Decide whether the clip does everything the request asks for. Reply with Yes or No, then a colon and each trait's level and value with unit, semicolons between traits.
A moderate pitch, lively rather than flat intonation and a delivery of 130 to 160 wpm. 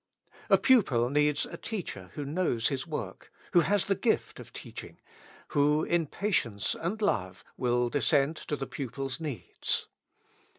Yes: medium, 145 Hz; wide, 5.8 semitones; average, 145 wpm